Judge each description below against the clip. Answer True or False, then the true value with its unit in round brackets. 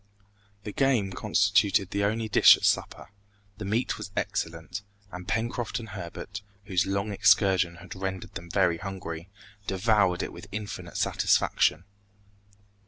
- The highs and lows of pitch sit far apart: False (2.5 semitones)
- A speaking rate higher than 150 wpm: False (135 wpm)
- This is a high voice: False (100 Hz)